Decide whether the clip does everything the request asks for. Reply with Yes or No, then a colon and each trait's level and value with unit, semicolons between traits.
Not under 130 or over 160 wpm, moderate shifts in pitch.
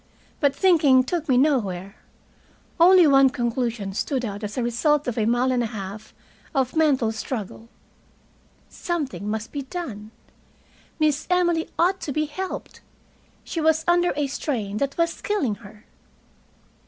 No: average, 145 wpm; wide, 6.2 semitones